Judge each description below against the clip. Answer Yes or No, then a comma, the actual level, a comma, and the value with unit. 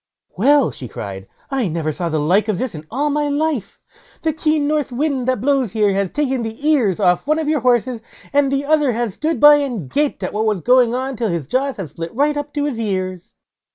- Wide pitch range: Yes, wide, 6.6 semitones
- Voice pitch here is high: Yes, very high, 255 Hz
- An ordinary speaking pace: No, fast, 230 wpm